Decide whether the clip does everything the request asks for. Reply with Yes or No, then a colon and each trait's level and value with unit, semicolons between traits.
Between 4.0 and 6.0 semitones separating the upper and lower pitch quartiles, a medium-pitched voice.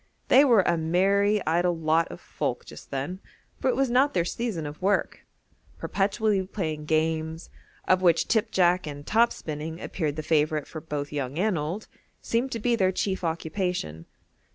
Yes: average, 4.5 semitones; medium, 175 Hz